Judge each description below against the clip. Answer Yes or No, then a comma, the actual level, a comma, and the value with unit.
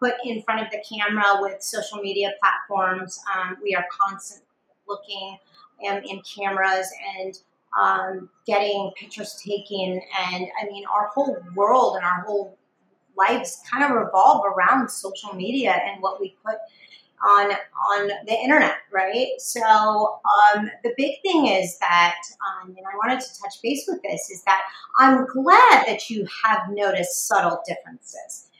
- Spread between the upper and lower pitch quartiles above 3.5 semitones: No, average, 3.0 semitones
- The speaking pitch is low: No, high, 205 Hz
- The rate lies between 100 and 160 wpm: Yes, average, 155 wpm